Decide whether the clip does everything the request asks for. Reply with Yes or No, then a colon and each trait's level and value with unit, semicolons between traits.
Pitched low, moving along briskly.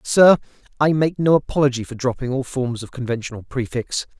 No: low, 130 Hz; average, 170 wpm